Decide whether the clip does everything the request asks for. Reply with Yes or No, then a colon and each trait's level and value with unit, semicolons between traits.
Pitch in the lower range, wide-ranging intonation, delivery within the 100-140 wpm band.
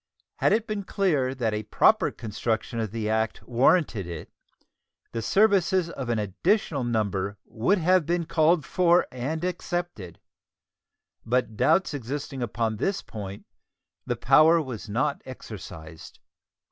Yes: low, 130 Hz; wide, 7.5 semitones; slow, 135 wpm